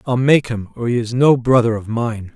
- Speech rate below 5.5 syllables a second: Yes, 5.1 syllables/s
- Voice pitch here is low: Yes, low, 120 Hz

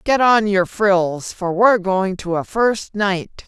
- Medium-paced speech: Yes, average, 190 wpm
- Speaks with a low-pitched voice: No, high, 200 Hz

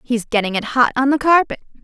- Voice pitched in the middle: No, very high, 255 Hz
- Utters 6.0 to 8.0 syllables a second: Yes, 6.1 syllables/s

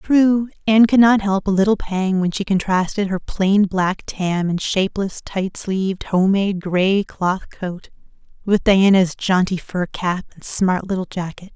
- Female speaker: Yes, female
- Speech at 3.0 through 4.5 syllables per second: Yes, 4.3 syllables/s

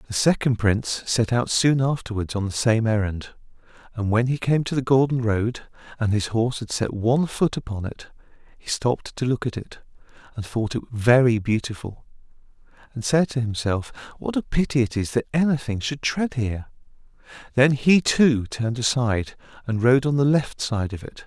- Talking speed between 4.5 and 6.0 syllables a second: Yes, 5.2 syllables/s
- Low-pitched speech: Yes, low, 120 Hz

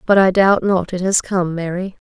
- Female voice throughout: Yes, female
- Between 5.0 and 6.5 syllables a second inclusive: No, 4.8 syllables/s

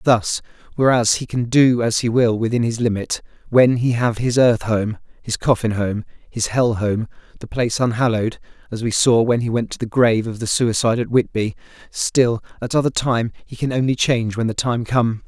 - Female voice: No, male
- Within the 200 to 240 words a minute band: Yes, fast, 205 wpm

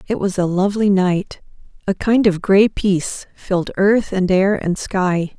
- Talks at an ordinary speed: Yes, average, 180 wpm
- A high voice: Yes, high, 195 Hz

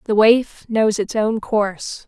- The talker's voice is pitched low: No, high, 215 Hz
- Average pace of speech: Yes, average, 175 wpm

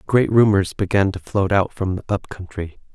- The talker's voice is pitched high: No, low, 100 Hz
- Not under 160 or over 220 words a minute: Yes, fast, 205 wpm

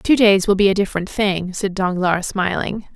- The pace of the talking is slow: No, fast, 205 wpm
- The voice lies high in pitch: Yes, high, 195 Hz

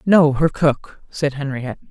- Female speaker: Yes, female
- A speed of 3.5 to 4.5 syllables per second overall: Yes, 4.3 syllables/s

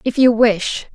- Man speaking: No, female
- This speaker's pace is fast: No, average, 190 wpm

